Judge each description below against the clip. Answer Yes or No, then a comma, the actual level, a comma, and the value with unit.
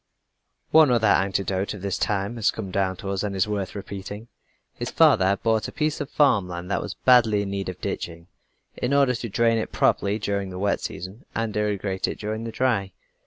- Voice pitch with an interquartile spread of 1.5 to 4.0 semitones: Yes, average, 2.8 semitones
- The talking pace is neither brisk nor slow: No, fast, 215 wpm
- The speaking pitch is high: No, low, 100 Hz